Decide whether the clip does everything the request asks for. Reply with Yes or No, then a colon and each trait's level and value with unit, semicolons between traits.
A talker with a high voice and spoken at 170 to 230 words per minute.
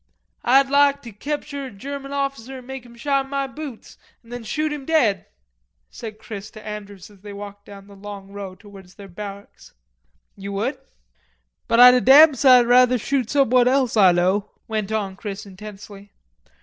Yes: high, 225 Hz; average, 175 wpm